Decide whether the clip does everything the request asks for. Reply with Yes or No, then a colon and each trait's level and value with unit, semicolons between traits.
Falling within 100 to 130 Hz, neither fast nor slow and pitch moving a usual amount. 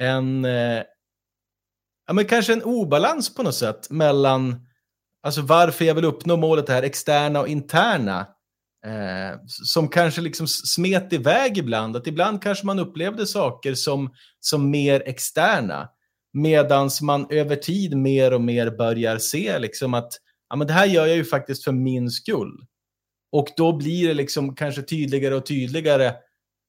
No: medium, 140 Hz; average, 155 wpm; average, 4.9 semitones